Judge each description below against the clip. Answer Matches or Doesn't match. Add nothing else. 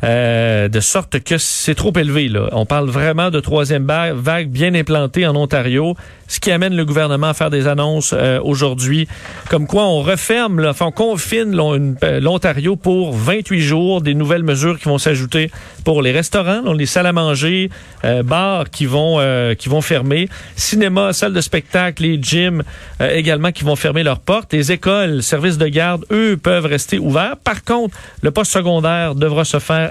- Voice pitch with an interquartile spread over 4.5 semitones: Doesn't match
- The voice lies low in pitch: Doesn't match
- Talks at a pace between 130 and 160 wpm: Doesn't match